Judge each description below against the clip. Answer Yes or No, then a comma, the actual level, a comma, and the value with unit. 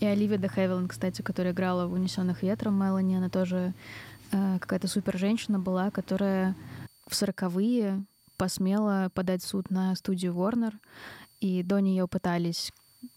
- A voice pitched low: No, high, 190 Hz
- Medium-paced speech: Yes, average, 135 wpm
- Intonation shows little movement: Yes, narrow, 1.3 semitones